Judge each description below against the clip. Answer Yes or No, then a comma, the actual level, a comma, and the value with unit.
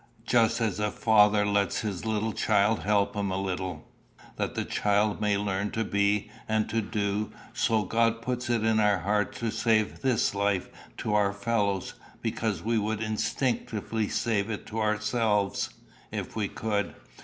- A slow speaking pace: No, average, 165 wpm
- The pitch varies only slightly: Yes, narrow, 1.7 semitones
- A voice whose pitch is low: Yes, low, 105 Hz